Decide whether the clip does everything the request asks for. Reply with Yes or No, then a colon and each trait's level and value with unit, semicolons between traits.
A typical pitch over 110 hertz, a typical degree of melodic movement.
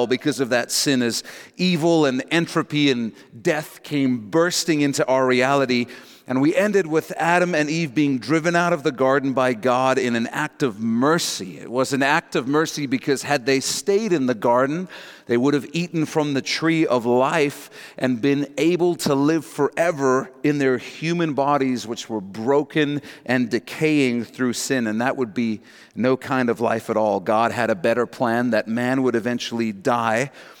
Yes: low, 135 Hz; average, 3.9 semitones